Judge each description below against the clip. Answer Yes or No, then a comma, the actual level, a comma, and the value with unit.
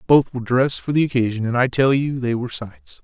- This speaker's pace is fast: Yes, fast, 255 wpm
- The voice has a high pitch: No, low, 125 Hz